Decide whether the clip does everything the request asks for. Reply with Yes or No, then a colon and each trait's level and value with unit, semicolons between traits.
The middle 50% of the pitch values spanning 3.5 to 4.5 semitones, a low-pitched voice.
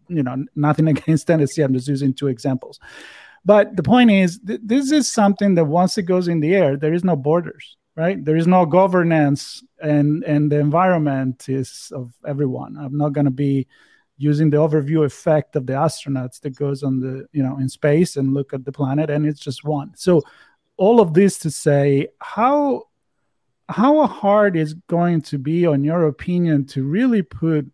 No: average, 4.1 semitones; medium, 150 Hz